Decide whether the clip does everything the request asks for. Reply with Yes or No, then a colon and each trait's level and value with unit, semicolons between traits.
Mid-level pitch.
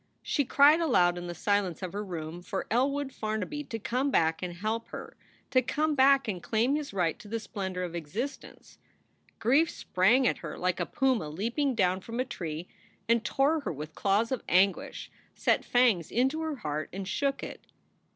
No: high, 220 Hz